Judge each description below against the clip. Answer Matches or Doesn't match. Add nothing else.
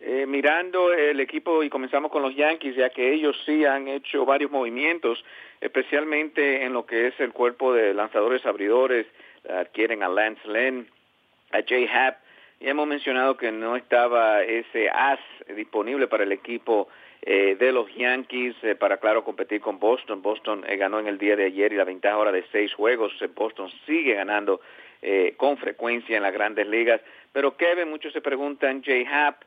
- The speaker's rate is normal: Matches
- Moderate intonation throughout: Matches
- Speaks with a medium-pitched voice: Doesn't match